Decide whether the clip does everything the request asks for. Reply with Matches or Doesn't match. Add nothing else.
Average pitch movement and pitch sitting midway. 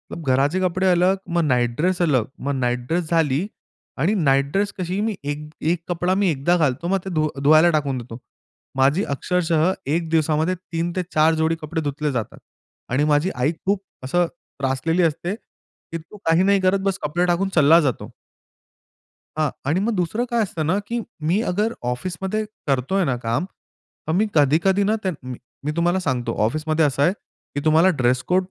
Matches